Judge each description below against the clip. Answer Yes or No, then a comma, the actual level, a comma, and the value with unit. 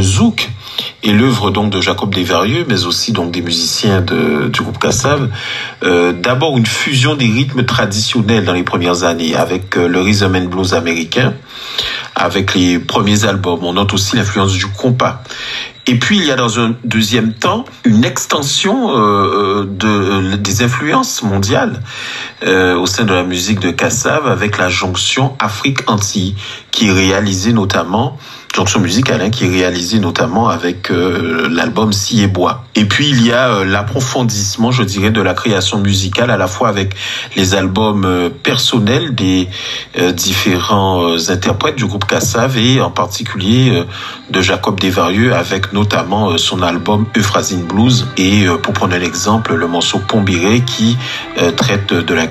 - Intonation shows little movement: No, average, 4.0 semitones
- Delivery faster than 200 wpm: No, average, 170 wpm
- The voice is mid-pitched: No, low, 105 Hz